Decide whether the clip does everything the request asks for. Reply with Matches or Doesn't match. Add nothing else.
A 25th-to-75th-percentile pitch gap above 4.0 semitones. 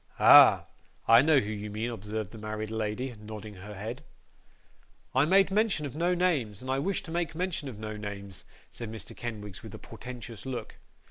Matches